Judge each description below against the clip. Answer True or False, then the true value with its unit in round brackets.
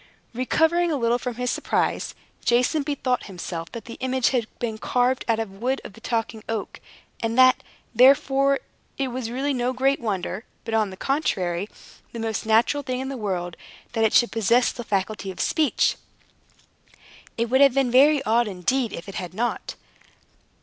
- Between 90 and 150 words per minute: False (180 wpm)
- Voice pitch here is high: True (240 Hz)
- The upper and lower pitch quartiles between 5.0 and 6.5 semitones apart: False (3.2 semitones)